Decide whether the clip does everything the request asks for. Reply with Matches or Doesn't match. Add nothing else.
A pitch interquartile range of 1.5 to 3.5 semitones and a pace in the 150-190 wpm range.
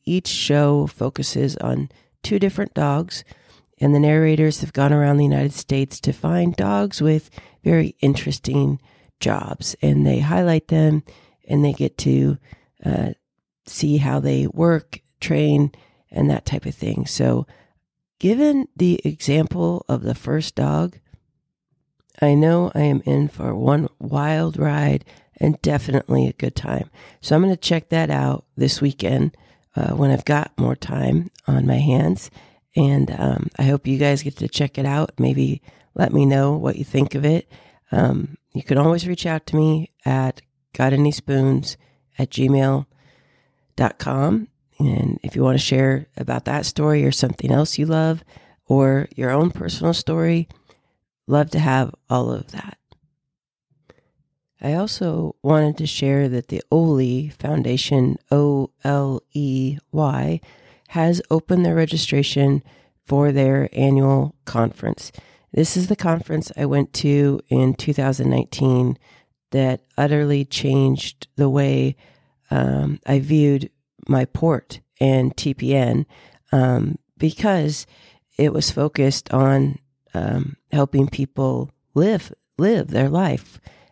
Doesn't match